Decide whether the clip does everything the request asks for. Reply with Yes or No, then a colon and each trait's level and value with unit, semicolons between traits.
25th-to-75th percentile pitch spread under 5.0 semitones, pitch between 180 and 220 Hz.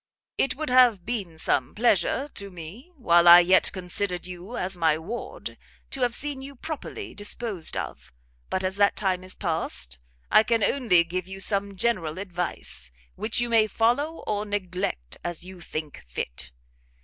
No: average, 5.3 semitones; high, 190 Hz